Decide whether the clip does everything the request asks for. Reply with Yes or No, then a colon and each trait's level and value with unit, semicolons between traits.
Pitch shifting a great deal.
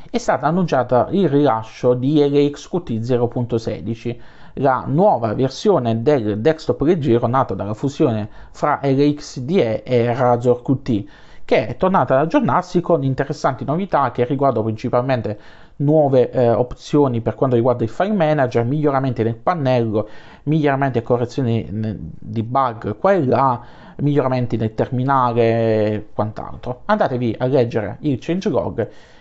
No: average, 3.9 semitones